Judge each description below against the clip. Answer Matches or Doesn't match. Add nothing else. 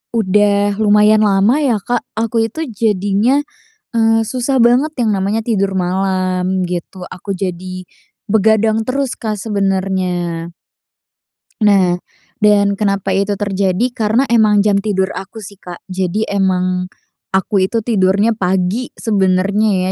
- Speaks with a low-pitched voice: Doesn't match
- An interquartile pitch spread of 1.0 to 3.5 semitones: Matches